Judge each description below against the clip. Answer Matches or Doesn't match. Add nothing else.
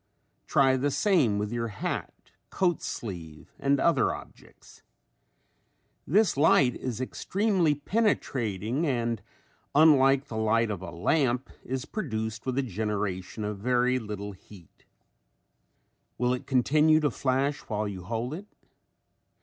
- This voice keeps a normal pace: Doesn't match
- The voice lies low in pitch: Matches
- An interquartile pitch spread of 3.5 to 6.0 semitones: Matches